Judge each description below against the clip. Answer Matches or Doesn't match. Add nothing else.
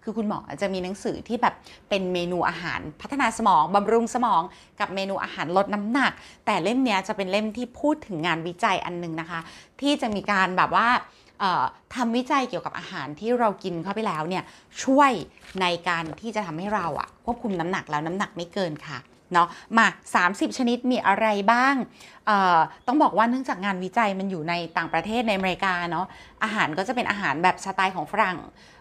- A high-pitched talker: Matches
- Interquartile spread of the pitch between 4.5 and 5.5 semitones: Matches